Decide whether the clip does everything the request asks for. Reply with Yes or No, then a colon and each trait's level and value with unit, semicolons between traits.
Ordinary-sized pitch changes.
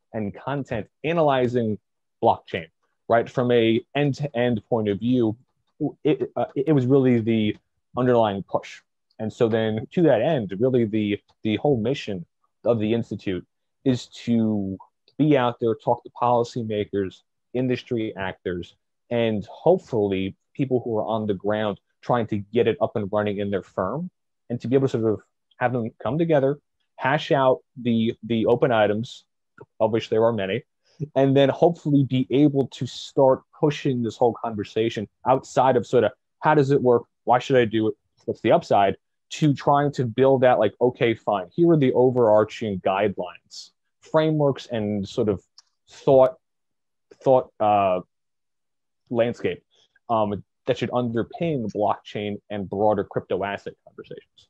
Yes: average, 3.9 semitones